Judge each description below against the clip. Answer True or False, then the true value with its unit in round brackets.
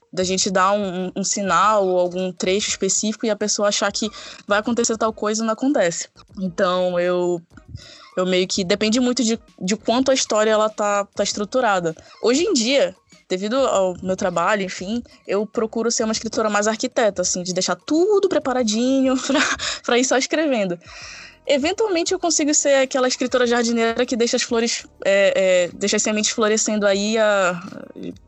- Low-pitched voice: False (215 Hz)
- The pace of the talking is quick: False (170 wpm)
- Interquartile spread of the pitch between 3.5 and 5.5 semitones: True (4.7 semitones)